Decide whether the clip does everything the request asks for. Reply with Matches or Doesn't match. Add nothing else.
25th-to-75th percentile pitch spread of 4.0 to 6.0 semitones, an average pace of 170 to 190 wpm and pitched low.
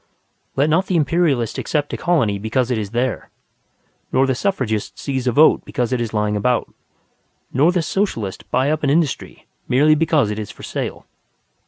Matches